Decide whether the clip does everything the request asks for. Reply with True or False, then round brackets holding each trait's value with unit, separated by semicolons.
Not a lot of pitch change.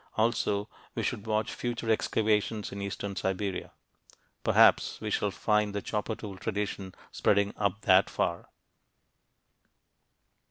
True (1.6 semitones)